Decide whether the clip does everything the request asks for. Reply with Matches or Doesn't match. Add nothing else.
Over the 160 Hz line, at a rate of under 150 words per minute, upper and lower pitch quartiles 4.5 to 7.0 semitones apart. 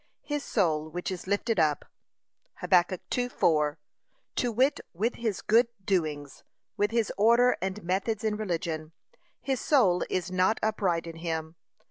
Matches